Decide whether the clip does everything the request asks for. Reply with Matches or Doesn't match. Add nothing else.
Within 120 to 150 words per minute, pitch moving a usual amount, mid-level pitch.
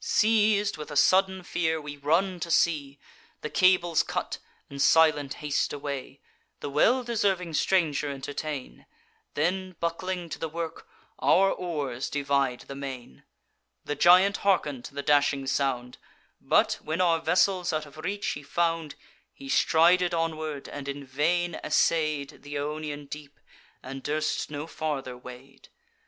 Matches